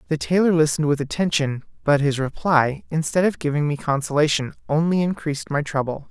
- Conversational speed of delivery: Yes, average, 165 wpm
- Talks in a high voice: No, medium, 150 Hz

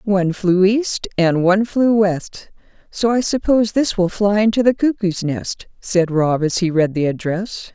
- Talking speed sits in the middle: Yes, average, 185 wpm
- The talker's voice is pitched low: No, high, 195 Hz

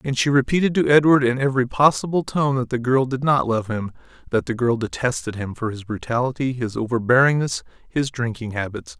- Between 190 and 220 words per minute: Yes, average, 195 wpm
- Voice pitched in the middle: No, low, 125 Hz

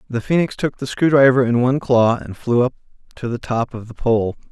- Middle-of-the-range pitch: No, low, 125 Hz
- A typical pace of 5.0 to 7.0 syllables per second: Yes, 5.6 syllables/s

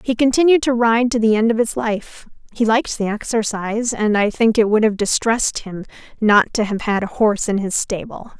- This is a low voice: No, high, 220 Hz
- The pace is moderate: No, fast, 220 wpm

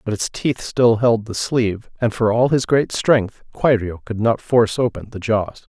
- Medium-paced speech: No, fast, 210 wpm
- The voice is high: No, low, 115 Hz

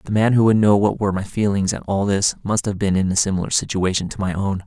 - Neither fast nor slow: No, fast, 285 wpm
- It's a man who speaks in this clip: Yes, male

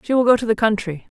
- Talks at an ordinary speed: No, fast, 305 wpm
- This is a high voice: Yes, high, 220 Hz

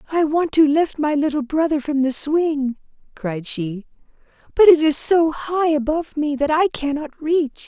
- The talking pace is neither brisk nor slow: Yes, average, 180 wpm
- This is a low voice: No, very high, 300 Hz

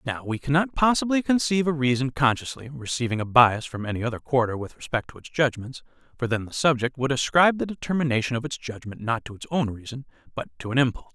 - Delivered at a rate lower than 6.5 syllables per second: No, 6.6 syllables/s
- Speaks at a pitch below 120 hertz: No, low, 135 Hz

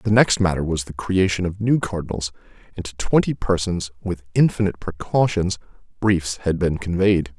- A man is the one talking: Yes, male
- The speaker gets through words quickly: No, average, 165 wpm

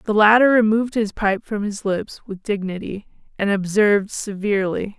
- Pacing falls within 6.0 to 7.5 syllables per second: No, 5.0 syllables/s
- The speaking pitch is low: No, high, 205 Hz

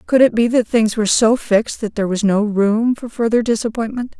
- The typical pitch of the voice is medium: No, high, 225 Hz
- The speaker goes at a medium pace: No, fast, 230 wpm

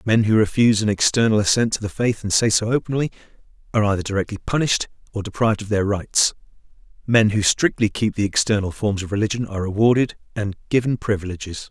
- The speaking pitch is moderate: No, low, 105 Hz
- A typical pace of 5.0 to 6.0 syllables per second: No, 6.5 syllables/s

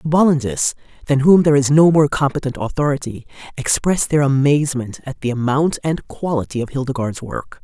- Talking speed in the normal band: Yes, average, 165 wpm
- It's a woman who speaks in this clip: Yes, female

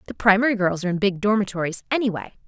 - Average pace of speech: Yes, average, 195 wpm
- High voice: Yes, high, 200 Hz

